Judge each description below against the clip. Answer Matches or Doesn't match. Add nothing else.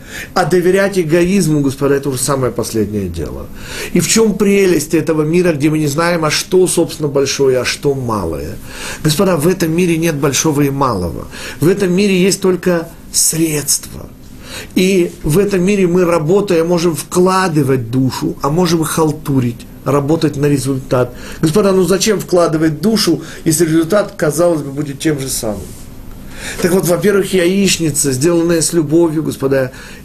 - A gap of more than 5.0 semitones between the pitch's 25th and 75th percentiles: Doesn't match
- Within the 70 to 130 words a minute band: Doesn't match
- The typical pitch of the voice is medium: Matches